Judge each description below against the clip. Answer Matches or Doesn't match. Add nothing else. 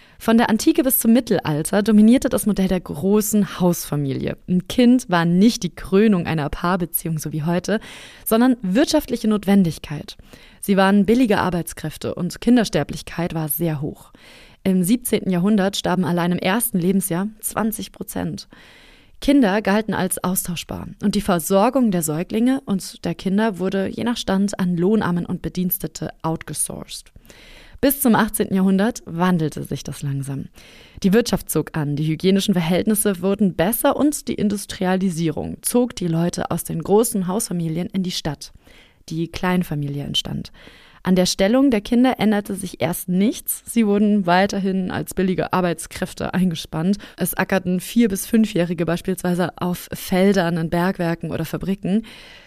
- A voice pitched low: Doesn't match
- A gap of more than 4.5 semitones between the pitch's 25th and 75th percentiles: Doesn't match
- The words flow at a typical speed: Matches